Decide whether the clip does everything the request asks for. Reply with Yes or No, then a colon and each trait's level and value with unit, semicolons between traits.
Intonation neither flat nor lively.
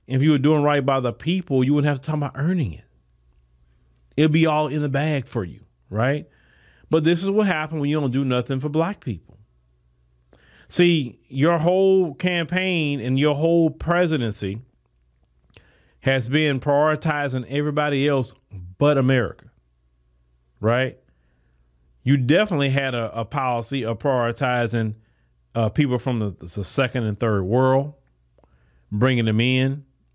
No: wide, 7.3 semitones